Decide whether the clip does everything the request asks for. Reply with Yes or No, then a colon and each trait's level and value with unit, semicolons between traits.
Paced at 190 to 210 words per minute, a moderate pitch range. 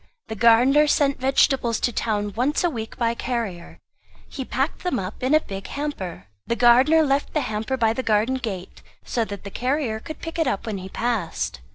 Yes: average, 195 wpm; average, 4.0 semitones